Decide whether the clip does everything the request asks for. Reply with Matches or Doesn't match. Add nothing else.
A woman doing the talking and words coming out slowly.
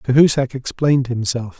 Doesn't match